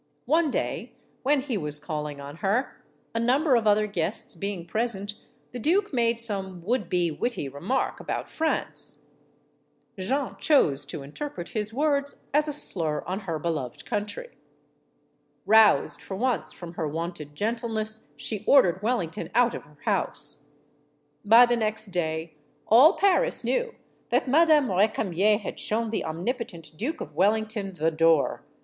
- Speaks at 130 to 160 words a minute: Yes, average, 150 wpm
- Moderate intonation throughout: No, wide, 6.6 semitones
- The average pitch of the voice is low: No, high, 210 Hz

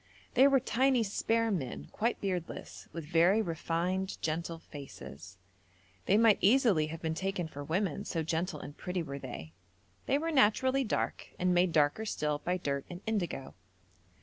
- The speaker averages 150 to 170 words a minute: Yes, average, 160 wpm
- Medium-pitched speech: Yes, medium, 180 Hz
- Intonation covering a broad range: Yes, wide, 5.7 semitones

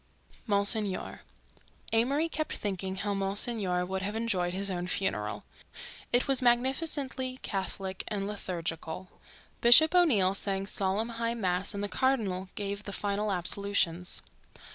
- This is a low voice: No, high, 200 Hz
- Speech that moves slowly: Yes, slow, 125 wpm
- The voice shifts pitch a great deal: No, average, 3.7 semitones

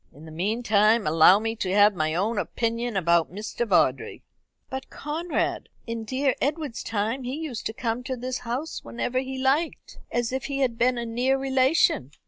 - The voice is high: Yes, high, 235 Hz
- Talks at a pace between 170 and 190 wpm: Yes, average, 180 wpm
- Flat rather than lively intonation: No, average, 4.2 semitones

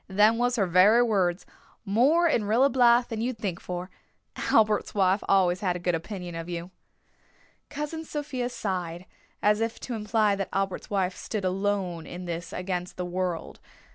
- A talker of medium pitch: No, high, 195 Hz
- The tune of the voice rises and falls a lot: No, average, 4.1 semitones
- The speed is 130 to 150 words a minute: No, average, 170 wpm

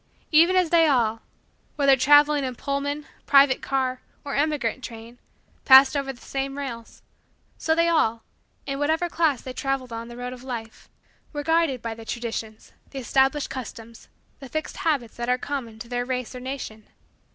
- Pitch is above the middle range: Yes, very high, 265 Hz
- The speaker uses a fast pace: No, average, 175 wpm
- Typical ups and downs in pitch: Yes, average, 3.3 semitones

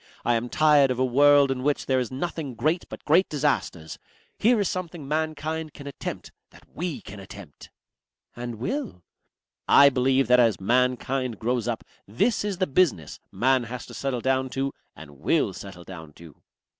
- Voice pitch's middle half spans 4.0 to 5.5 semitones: Yes, average, 4.5 semitones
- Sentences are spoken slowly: No, average, 175 wpm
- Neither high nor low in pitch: No, low, 130 Hz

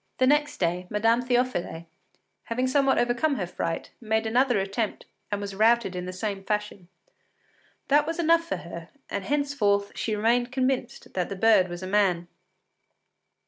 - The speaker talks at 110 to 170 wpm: Yes, average, 160 wpm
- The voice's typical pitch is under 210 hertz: No, high, 220 Hz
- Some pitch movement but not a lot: Yes, average, 4.9 semitones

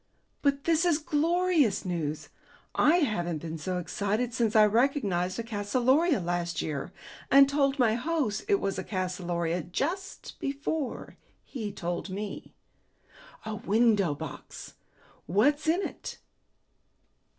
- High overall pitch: Yes, high, 220 Hz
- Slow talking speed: Yes, slow, 125 wpm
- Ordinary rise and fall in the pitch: No, wide, 8.0 semitones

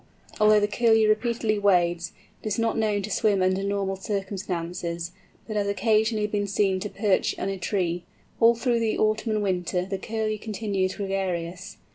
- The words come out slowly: No, average, 170 wpm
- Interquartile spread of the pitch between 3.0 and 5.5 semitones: No, narrow, 2.4 semitones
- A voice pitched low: No, high, 200 Hz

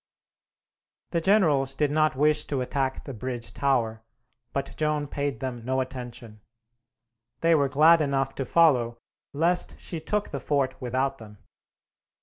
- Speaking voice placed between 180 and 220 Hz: No, low, 135 Hz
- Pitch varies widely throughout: No, average, 3.0 semitones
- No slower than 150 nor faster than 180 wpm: No, average, 140 wpm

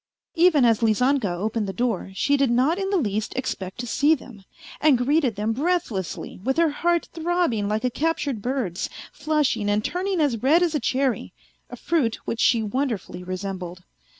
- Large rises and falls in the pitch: Yes, wide, 6.5 semitones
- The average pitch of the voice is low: No, very high, 250 Hz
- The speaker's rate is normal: Yes, average, 180 wpm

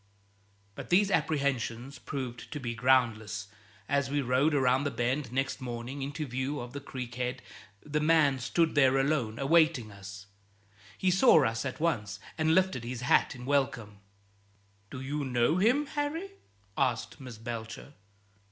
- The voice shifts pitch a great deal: No, average, 4.0 semitones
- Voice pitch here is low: Yes, low, 130 Hz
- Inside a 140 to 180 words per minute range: Yes, average, 150 wpm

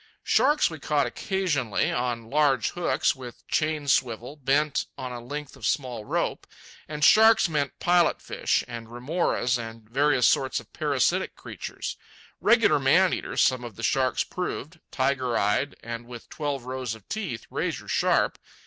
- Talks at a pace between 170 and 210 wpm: No, average, 155 wpm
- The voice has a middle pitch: No, low, 130 Hz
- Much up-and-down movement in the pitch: No, average, 3.9 semitones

